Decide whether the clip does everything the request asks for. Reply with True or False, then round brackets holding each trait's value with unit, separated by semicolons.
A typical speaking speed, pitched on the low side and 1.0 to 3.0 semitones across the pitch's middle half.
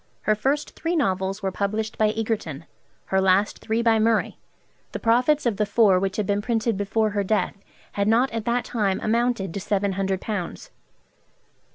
False (180 wpm; 215 Hz; 2.7 semitones)